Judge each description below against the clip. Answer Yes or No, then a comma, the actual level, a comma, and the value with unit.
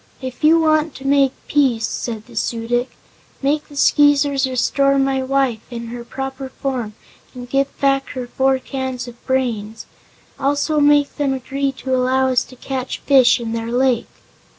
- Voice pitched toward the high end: Yes, very high, 265 Hz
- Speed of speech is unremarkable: Yes, average, 170 wpm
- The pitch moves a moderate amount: No, narrow, 2.1 semitones